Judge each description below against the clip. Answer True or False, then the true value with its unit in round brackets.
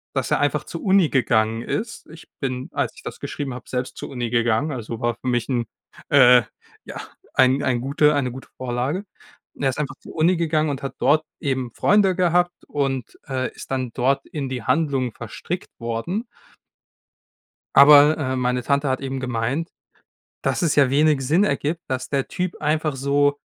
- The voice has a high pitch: False (135 Hz)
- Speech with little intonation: False (3.5 semitones)